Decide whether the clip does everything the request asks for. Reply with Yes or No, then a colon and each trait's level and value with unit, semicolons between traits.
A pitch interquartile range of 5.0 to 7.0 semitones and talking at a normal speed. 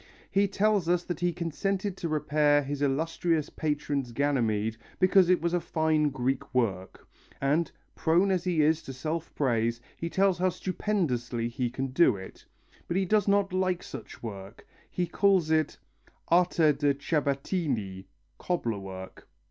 Yes: average, 5.3 semitones; average, 155 wpm